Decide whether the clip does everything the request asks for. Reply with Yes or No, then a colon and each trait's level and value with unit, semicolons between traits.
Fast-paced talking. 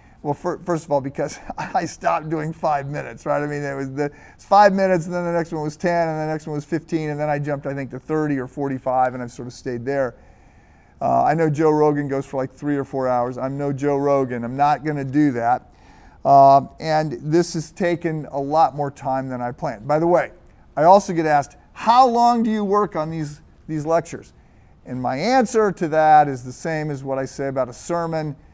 Yes: fast, 240 wpm